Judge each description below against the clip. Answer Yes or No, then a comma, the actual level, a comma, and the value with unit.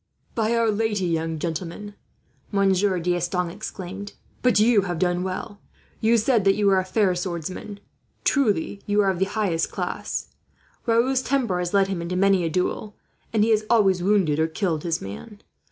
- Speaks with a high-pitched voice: Yes, high, 195 Hz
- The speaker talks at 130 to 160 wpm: No, average, 175 wpm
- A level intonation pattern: No, average, 3.1 semitones